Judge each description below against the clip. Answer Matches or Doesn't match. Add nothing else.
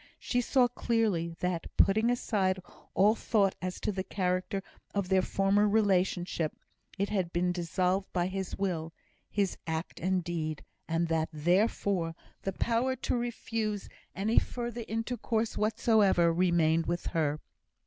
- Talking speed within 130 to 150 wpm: Matches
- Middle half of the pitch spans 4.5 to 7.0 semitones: Doesn't match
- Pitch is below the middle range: Doesn't match